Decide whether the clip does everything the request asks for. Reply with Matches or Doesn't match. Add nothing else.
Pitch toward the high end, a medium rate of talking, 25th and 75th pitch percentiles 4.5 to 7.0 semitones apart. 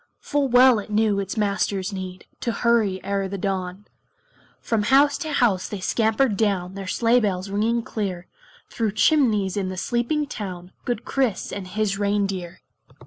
Doesn't match